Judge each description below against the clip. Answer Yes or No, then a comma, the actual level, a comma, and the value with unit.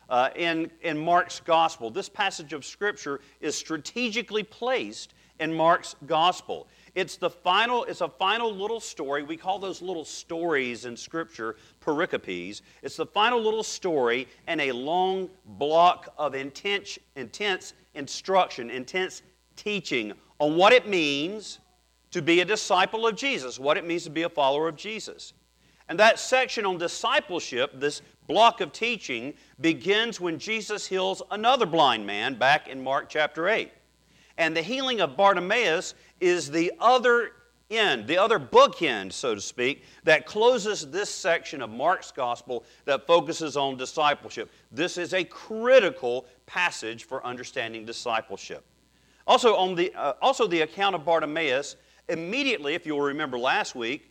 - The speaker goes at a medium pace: Yes, average, 150 wpm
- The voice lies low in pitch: No, medium, 170 Hz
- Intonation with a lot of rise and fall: Yes, wide, 6.1 semitones